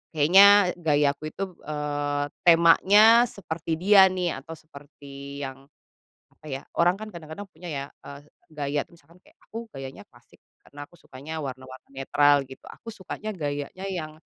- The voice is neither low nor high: Yes, medium, 155 Hz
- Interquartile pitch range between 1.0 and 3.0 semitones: No, average, 4.3 semitones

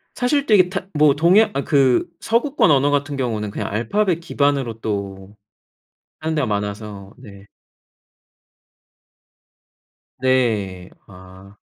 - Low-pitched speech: Yes, low, 130 Hz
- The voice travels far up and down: Yes, wide, 7.5 semitones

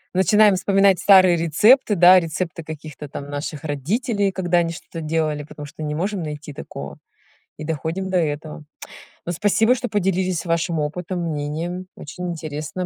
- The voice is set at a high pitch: No, medium, 170 Hz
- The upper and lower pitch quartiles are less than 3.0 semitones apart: No, average, 3.6 semitones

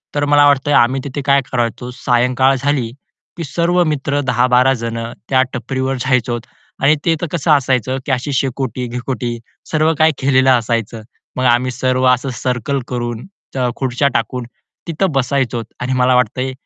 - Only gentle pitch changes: Yes, narrow, 2.1 semitones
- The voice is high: No, low, 130 Hz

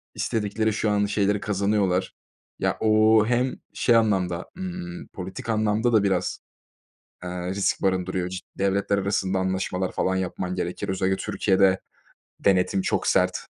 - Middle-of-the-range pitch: No, low, 100 Hz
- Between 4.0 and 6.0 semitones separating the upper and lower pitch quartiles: No, narrow, 2.4 semitones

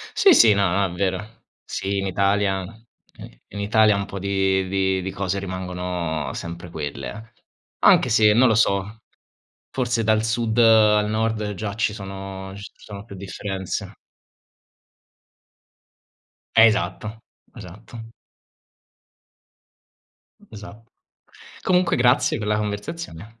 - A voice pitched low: Yes, low, 100 Hz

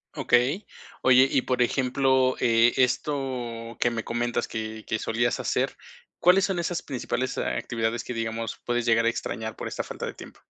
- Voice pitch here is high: No, low, 120 Hz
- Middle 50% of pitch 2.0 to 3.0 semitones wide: Yes, narrow, 2.4 semitones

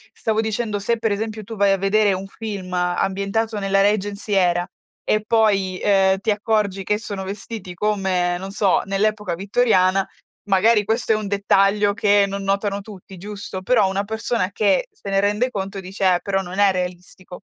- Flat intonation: Yes, narrow, 1.8 semitones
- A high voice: Yes, high, 200 Hz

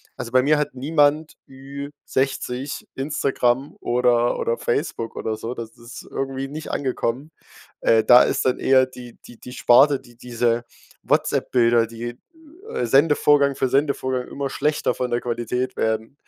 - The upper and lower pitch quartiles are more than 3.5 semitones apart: No, average, 2.7 semitones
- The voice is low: Yes, low, 130 Hz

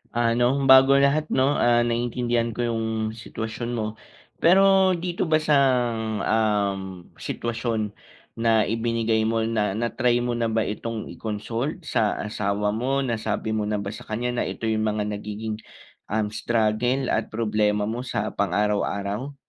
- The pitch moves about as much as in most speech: No, narrow, 2.2 semitones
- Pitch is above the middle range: No, low, 115 Hz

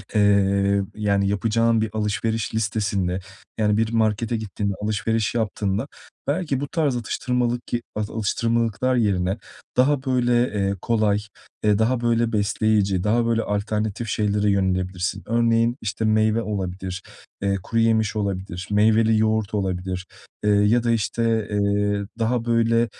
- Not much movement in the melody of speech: Yes, narrow, 2.3 semitones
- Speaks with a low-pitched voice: Yes, low, 110 Hz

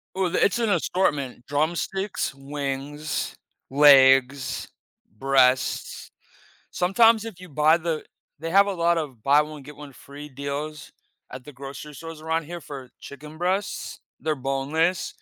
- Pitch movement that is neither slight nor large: Yes, average, 3.7 semitones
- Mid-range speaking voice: Yes, medium, 150 Hz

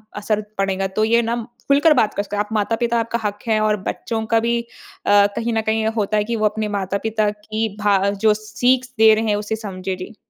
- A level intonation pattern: Yes, narrow, 1.7 semitones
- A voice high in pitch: Yes, high, 215 Hz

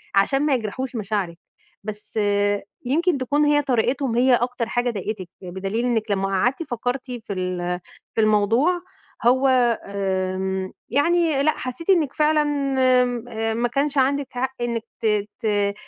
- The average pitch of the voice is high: Yes, high, 240 Hz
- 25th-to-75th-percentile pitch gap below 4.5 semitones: No, average, 4.9 semitones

